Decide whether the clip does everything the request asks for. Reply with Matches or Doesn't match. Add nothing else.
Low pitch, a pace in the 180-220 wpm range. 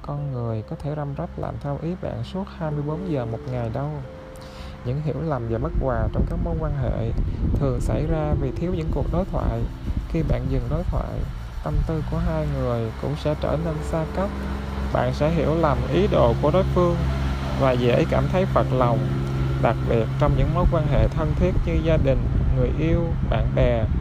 Matches